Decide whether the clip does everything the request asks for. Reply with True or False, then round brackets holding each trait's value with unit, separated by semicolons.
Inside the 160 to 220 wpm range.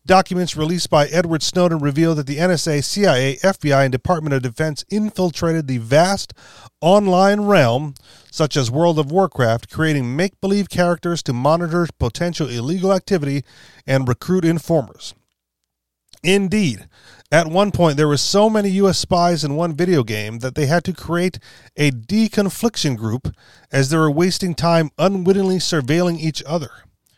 False (150 wpm)